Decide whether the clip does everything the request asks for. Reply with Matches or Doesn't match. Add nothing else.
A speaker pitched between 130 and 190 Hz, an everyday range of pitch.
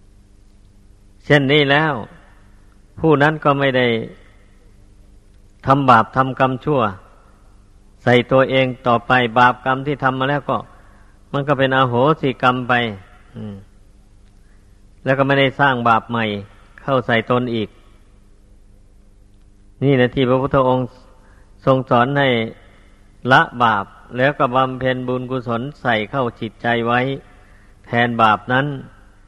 Doesn't match